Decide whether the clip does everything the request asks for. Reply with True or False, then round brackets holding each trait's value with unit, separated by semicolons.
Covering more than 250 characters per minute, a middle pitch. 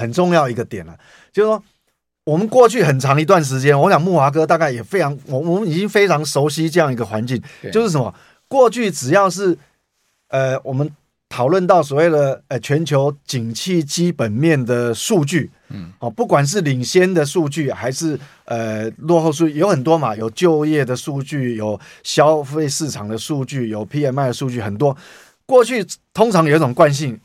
True (275 characters per minute; 150 Hz)